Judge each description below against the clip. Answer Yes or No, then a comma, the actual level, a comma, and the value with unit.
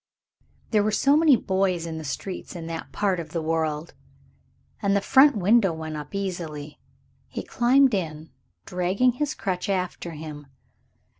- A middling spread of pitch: Yes, average, 4.3 semitones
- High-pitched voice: No, medium, 180 Hz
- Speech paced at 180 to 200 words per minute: No, average, 155 wpm